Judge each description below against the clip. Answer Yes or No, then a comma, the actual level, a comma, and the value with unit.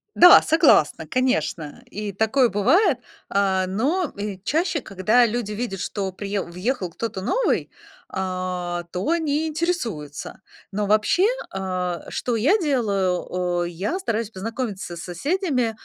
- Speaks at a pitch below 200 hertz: No, high, 210 Hz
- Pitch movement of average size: No, wide, 6.3 semitones